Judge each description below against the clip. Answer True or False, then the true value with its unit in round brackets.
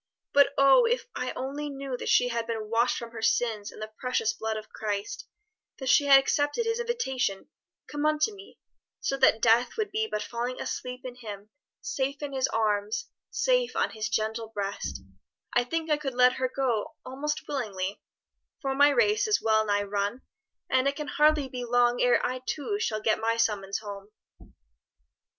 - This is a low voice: False (250 Hz)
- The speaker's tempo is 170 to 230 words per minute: True (185 wpm)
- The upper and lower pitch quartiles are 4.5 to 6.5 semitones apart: True (4.8 semitones)